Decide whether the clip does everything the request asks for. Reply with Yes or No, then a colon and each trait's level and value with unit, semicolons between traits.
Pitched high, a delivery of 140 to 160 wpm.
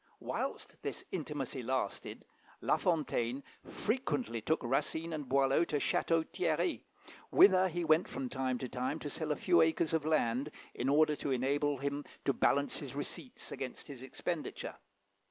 No: medium, 145 Hz; average, 155 wpm